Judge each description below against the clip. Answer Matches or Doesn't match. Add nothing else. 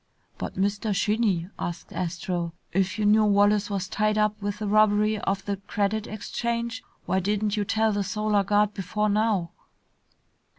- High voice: Matches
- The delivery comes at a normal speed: Matches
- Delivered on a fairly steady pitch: Matches